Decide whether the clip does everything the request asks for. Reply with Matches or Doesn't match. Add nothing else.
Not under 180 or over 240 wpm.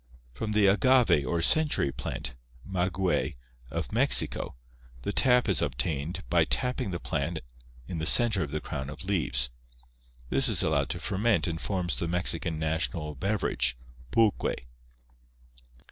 Doesn't match